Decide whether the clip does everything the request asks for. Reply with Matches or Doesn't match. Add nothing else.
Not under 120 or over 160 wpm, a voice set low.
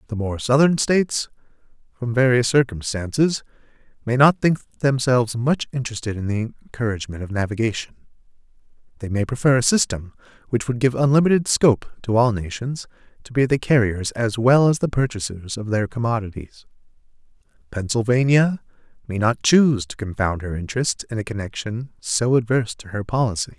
Matches